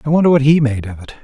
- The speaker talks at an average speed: No, fast, 340 wpm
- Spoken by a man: Yes, male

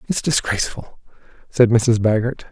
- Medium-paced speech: No, slow, 120 wpm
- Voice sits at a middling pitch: No, low, 120 Hz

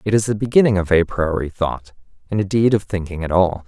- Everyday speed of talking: No, fast, 230 wpm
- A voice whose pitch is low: Yes, very low, 95 Hz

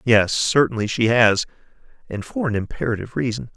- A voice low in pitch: Yes, low, 115 Hz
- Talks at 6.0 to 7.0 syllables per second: No, 5.7 syllables/s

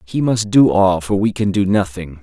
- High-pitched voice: No, low, 100 Hz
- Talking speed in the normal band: No, fast, 245 wpm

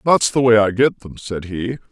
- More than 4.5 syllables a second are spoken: Yes, 4.8 syllables/s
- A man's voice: Yes, male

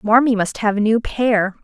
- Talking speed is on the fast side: Yes, fast, 220 wpm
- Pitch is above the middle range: Yes, high, 220 Hz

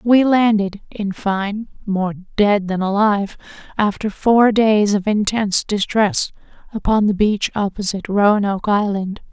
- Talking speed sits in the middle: No, slow, 130 wpm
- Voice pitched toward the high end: Yes, high, 205 Hz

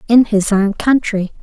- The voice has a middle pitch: No, high, 215 Hz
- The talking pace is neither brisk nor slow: Yes, average, 170 wpm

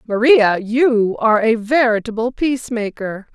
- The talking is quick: No, slow, 125 wpm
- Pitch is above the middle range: Yes, high, 230 Hz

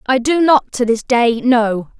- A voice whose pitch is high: Yes, very high, 250 Hz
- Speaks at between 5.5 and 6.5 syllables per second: No, 3.8 syllables/s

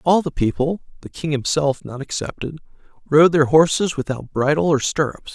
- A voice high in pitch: No, medium, 155 Hz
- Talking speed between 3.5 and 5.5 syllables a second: Yes, 5.0 syllables/s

